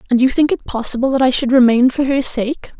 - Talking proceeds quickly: Yes, fast, 255 wpm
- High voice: Yes, very high, 255 Hz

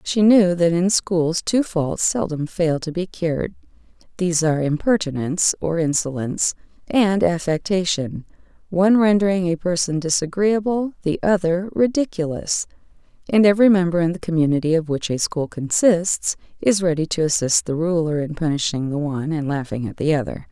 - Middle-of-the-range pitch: Yes, medium, 170 Hz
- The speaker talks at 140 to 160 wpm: Yes, average, 150 wpm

